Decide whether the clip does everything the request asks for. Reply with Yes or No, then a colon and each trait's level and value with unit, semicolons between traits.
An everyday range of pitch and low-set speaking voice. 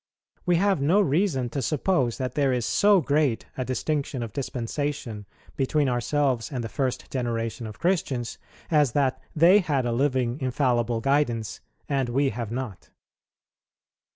Yes: average, 3.6 semitones; low, 130 Hz